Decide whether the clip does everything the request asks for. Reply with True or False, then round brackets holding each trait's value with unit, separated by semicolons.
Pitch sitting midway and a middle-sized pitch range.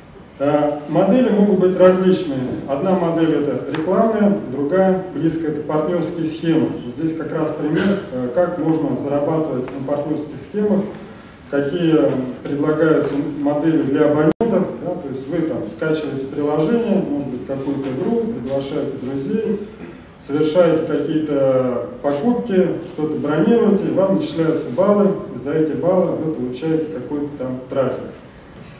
True (155 Hz; 4.3 semitones)